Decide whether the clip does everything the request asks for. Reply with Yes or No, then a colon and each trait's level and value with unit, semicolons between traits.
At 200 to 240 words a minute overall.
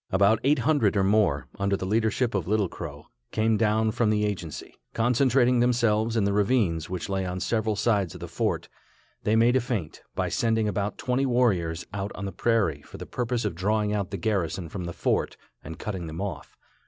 Yes: fast, 205 wpm